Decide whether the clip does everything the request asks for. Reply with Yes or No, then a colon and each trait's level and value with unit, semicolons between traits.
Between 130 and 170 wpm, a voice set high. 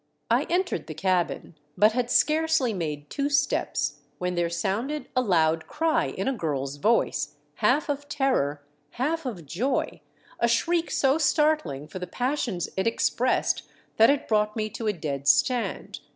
Yes: average, 165 wpm; high, 220 Hz